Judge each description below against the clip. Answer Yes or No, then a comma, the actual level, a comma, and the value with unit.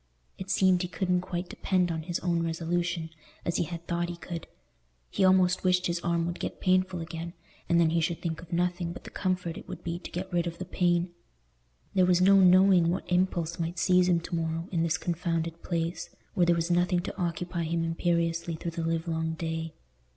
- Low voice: No, medium, 170 Hz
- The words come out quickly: Yes, fast, 210 wpm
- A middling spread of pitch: No, narrow, 1.3 semitones